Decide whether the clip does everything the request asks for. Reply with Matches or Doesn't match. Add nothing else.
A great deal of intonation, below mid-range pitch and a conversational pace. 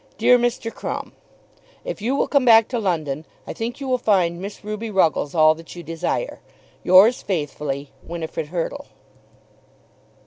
Doesn't match